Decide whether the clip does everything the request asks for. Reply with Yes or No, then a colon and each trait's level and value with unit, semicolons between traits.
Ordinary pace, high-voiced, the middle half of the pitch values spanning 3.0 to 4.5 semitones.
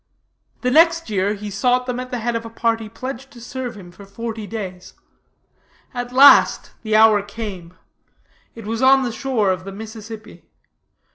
Yes: average, 170 wpm; high, 225 Hz; average, 3.4 semitones